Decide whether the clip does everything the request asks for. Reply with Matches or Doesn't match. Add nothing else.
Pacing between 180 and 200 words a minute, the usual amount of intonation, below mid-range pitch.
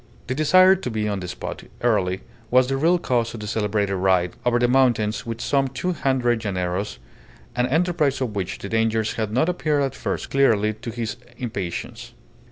Matches